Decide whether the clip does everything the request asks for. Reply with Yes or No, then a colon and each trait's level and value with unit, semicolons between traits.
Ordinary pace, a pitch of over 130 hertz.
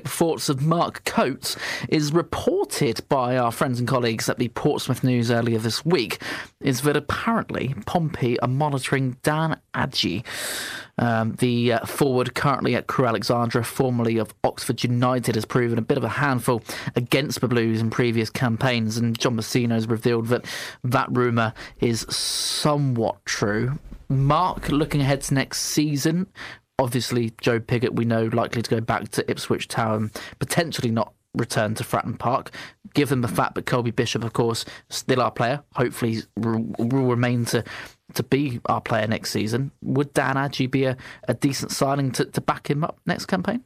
No: average, 170 wpm; low, 125 Hz